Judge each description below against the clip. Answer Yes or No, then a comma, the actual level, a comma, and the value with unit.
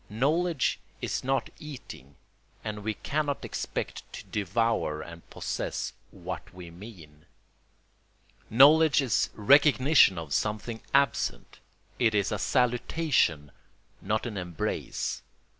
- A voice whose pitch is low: Yes, low, 110 Hz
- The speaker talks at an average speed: No, slow, 110 wpm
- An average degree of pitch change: No, wide, 7.0 semitones